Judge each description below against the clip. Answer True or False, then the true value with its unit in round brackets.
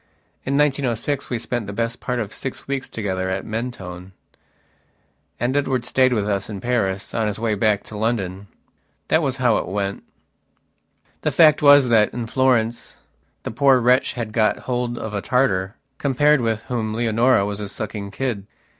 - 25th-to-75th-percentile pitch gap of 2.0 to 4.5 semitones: True (3.8 semitones)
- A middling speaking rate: True (170 wpm)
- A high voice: False (115 Hz)